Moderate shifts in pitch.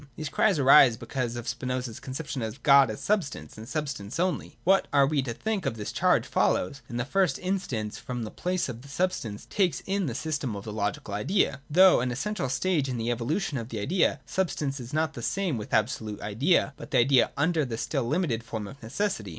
No: wide, 5.9 semitones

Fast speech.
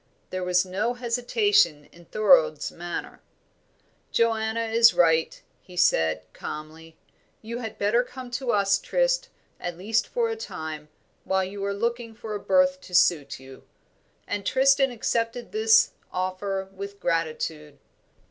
No: average, 140 wpm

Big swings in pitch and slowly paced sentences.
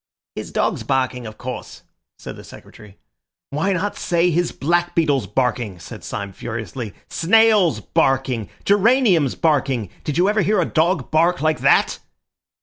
No: wide, 6.2 semitones; average, 145 wpm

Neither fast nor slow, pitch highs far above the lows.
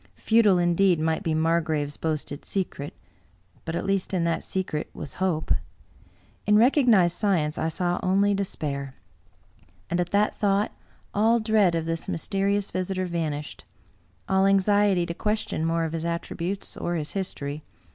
No: average, 160 wpm; average, 3.5 semitones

